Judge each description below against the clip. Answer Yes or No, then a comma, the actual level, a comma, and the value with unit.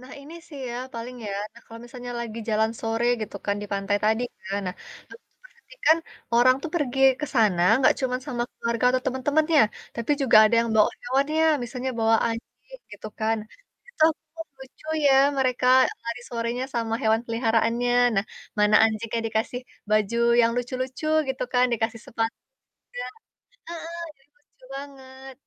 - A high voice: Yes, high, 240 Hz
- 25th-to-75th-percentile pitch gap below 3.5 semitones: Yes, average, 2.9 semitones